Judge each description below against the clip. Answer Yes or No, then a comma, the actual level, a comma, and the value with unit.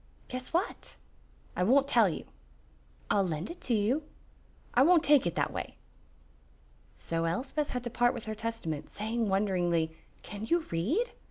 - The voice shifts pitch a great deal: Yes, wide, 6.5 semitones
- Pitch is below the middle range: No, high, 225 Hz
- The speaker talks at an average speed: Yes, average, 160 wpm